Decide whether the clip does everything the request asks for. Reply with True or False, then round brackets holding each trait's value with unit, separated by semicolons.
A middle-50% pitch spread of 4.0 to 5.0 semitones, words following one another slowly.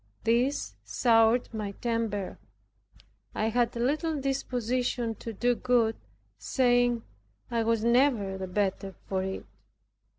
False (2.4 semitones; 110 wpm)